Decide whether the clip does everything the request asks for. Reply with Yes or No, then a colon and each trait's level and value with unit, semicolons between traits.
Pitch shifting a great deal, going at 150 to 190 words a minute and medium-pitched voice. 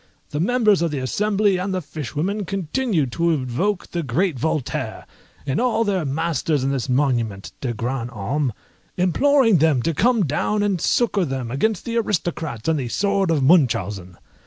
Yes: wide, 7.1 semitones; average, 165 wpm; medium, 160 Hz